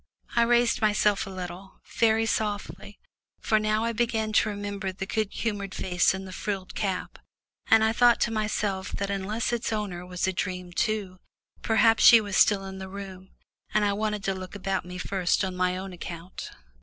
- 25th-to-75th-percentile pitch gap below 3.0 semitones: Yes, narrow, 2.5 semitones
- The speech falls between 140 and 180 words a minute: No, average, 190 wpm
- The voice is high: Yes, high, 200 Hz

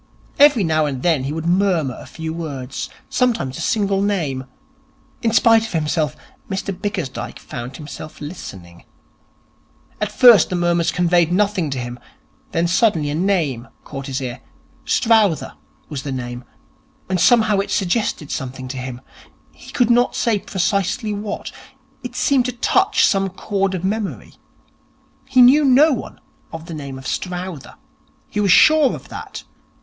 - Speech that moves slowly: No, average, 155 wpm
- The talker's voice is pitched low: No, medium, 180 Hz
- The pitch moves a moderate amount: No, wide, 6.5 semitones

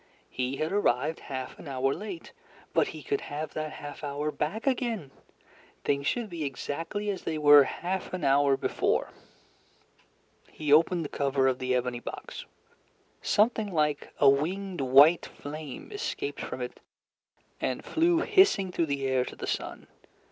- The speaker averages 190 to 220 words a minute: No, average, 155 wpm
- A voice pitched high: No, medium, 150 Hz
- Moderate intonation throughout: No, wide, 5.9 semitones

